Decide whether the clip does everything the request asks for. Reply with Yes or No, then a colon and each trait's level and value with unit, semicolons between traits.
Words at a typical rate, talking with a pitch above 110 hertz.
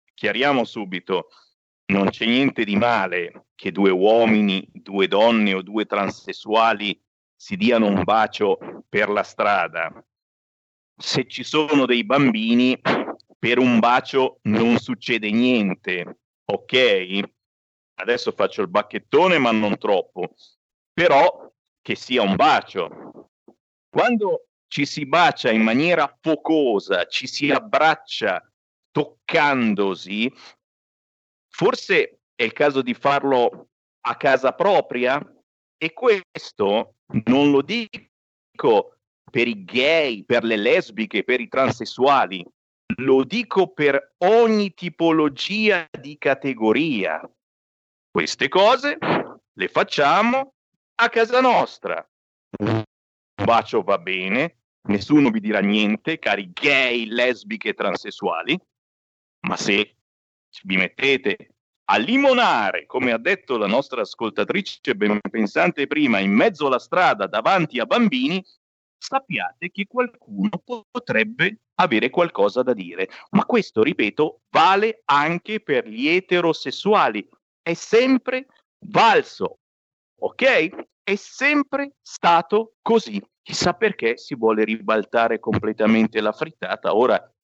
No: slow, 110 wpm; medium, 140 Hz